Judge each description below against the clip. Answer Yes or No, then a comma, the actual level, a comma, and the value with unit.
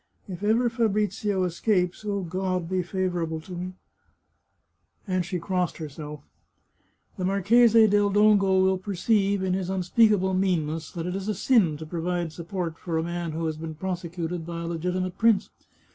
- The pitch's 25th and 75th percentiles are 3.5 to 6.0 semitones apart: No, average, 2.7 semitones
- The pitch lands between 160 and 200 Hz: Yes, medium, 185 Hz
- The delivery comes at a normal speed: Yes, average, 170 wpm